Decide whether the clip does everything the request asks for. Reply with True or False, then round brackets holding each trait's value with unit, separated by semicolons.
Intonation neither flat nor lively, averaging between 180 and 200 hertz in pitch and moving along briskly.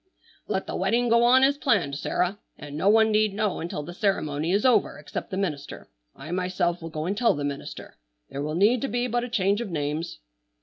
False (6.3 semitones; 190 Hz; 220 wpm)